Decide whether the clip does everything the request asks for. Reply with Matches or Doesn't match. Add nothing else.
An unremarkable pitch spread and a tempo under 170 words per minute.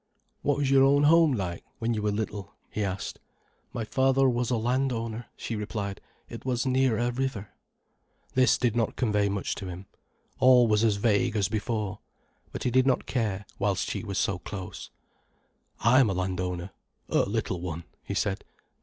Doesn't match